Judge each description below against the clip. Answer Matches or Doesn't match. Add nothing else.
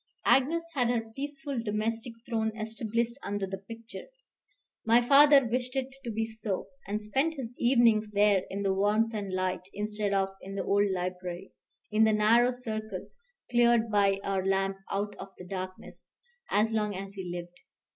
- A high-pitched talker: Matches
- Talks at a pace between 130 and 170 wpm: Matches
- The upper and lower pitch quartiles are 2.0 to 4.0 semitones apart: Matches